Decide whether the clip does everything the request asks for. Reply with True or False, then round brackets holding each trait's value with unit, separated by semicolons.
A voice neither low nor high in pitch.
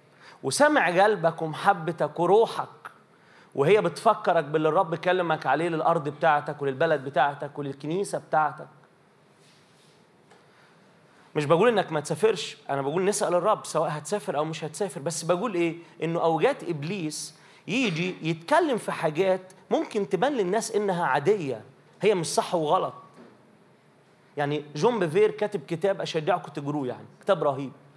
True (170 Hz)